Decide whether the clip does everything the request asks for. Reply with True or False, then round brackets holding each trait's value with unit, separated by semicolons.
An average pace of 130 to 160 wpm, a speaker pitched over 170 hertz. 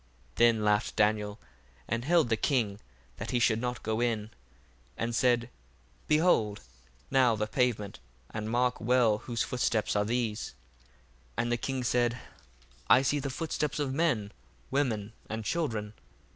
False (150 wpm; 115 Hz)